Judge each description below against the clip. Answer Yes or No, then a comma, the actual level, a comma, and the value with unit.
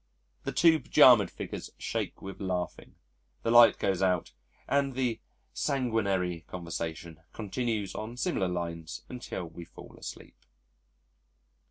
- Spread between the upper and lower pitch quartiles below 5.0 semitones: No, wide, 5.6 semitones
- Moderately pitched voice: No, low, 100 Hz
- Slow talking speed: Yes, slow, 125 wpm